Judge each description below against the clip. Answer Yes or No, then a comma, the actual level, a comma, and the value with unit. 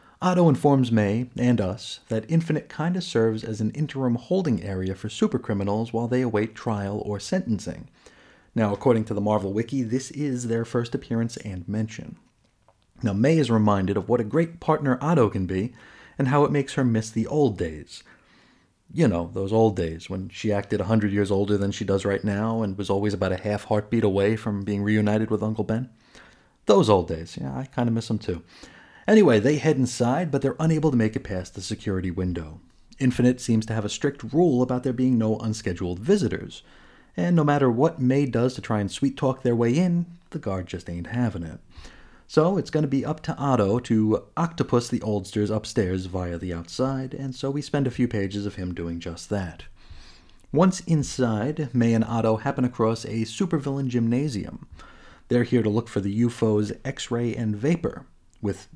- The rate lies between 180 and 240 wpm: Yes, average, 195 wpm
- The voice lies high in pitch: No, low, 115 Hz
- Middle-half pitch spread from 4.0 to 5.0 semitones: Yes, average, 4.6 semitones